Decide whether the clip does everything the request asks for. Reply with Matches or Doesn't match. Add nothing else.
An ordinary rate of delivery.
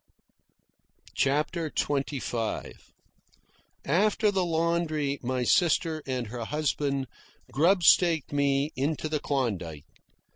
Doesn't match